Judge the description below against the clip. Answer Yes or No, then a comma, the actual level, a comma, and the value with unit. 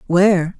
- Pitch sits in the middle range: Yes, medium, 180 Hz